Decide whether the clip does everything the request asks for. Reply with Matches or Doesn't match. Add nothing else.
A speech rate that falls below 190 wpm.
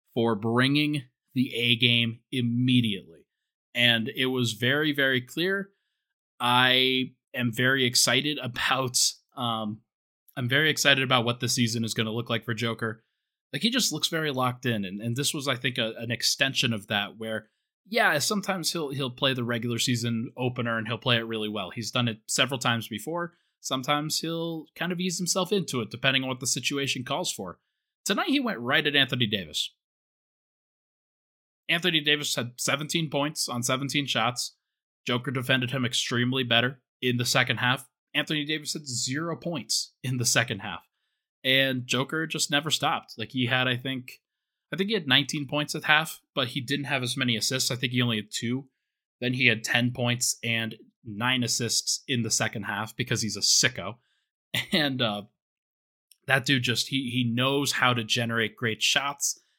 Matches